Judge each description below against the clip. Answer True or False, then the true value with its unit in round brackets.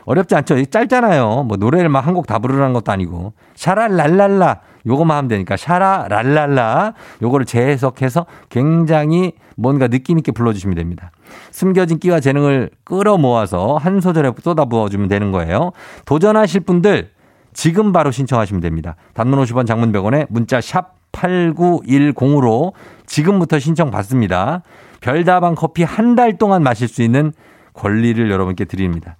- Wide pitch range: True (7.5 semitones)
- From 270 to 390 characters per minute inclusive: True (335 characters per minute)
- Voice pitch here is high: False (140 Hz)